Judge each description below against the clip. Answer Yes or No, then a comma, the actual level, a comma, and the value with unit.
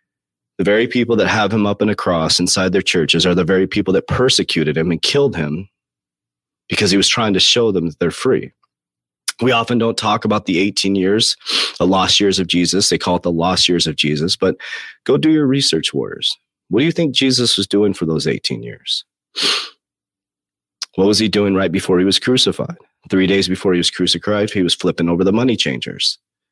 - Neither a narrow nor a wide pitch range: Yes, average, 3.4 semitones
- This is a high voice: No, very low, 95 Hz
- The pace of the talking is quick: Yes, fast, 210 wpm